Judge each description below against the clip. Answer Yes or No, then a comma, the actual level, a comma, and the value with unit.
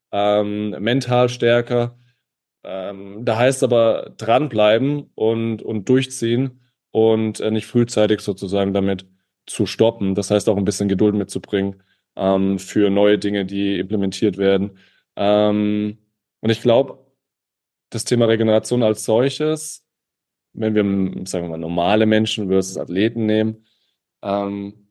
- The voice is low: Yes, low, 105 Hz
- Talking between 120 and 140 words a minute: Yes, average, 130 wpm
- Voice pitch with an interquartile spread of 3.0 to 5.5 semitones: No, narrow, 2.4 semitones